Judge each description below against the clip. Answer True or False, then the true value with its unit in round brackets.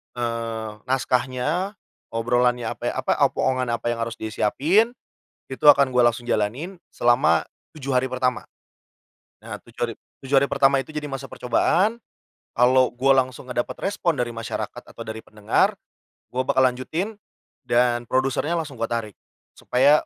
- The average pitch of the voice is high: False (125 Hz)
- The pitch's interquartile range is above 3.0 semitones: False (2.7 semitones)